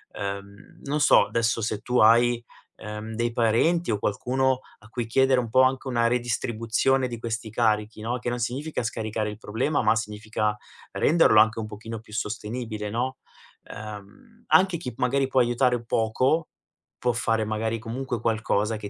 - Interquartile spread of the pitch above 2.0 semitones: Yes, narrow, 2.6 semitones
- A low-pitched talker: Yes, low, 115 Hz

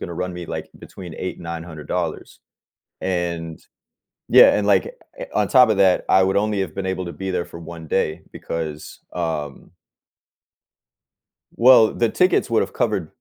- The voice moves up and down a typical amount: Yes, average, 3.5 semitones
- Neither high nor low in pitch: No, very low, 90 Hz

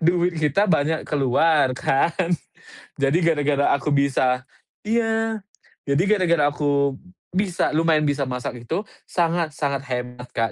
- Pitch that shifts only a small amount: No, average, 3.8 semitones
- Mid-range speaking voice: Yes, medium, 150 Hz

